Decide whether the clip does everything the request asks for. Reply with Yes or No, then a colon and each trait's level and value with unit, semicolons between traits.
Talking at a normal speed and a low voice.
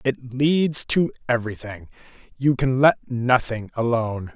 No: slow, 125 wpm; low, 125 Hz